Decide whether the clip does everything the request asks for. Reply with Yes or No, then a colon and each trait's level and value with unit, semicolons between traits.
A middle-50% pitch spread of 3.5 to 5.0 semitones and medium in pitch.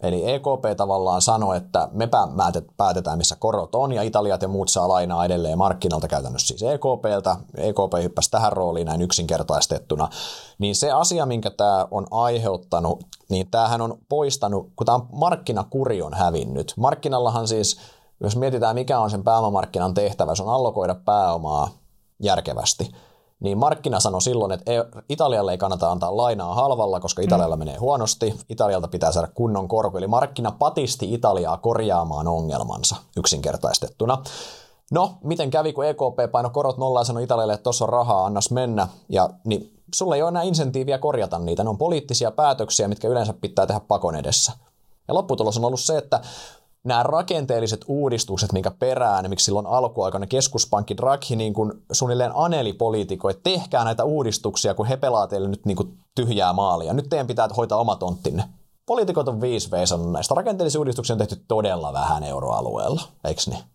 No: average, 4.6 semitones; low, 110 Hz